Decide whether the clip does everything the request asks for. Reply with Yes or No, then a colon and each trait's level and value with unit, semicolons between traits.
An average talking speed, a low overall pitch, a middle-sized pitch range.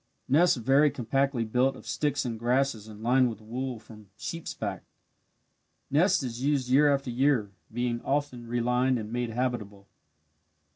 Yes: average, 150 wpm; low, 125 Hz; average, 3.0 semitones